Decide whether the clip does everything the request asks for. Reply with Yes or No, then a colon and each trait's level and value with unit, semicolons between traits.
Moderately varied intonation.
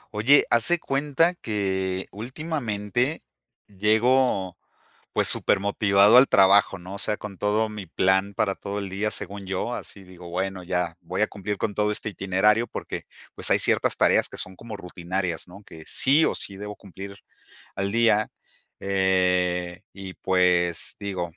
No: narrow, 2.3 semitones